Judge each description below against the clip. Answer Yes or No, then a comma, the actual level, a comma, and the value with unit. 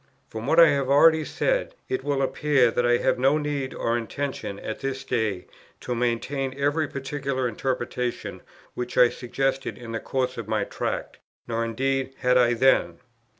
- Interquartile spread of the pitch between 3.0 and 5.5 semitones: No, narrow, 2.6 semitones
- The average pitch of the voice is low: Yes, low, 130 Hz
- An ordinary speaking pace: Yes, average, 170 wpm